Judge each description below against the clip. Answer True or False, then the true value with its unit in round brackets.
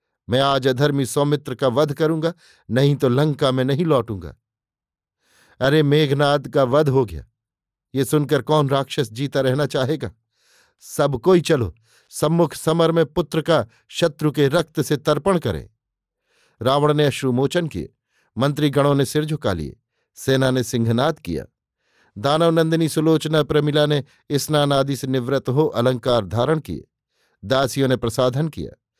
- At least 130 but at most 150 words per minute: True (145 wpm)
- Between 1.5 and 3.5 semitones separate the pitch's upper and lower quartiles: True (2.9 semitones)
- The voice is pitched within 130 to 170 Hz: True (140 Hz)